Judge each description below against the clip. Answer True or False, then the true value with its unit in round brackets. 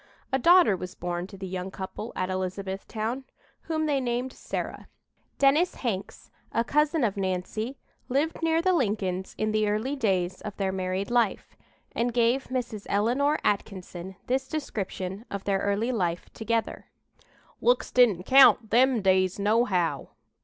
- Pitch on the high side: True (215 Hz)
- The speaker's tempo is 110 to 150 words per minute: True (145 wpm)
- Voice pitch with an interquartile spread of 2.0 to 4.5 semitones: False (5.3 semitones)